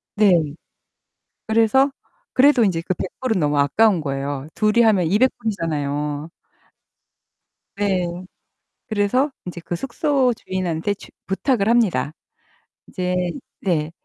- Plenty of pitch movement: Yes, wide, 5.7 semitones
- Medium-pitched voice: No, high, 195 Hz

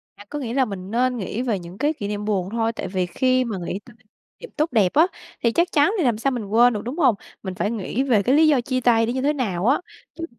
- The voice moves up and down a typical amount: Yes, average, 4.7 semitones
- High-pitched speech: Yes, high, 235 Hz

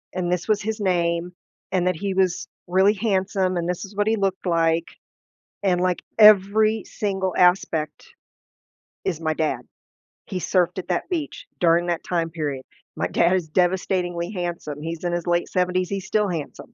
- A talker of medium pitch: Yes, medium, 180 Hz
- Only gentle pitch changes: Yes, narrow, 2.2 semitones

